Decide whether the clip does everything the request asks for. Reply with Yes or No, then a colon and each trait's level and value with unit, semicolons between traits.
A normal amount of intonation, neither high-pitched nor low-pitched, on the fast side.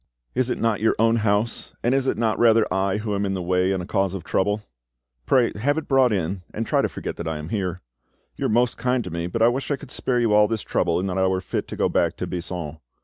No: average, 4.0 semitones; low, 105 Hz; fast, 280 wpm